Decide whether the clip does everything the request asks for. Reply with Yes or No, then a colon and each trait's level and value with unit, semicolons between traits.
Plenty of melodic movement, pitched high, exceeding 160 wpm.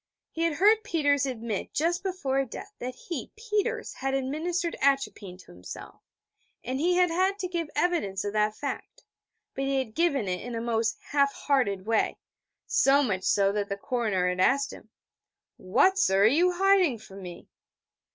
Yes: wide, 8.3 semitones; very high, 270 Hz; average, 175 wpm